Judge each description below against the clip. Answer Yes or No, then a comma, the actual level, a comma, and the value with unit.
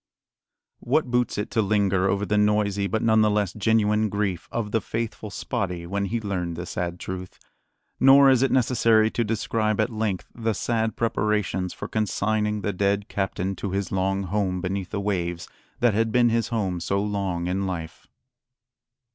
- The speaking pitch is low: Yes, low, 105 Hz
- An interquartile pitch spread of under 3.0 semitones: Yes, narrow, 2.6 semitones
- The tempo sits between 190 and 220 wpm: No, average, 175 wpm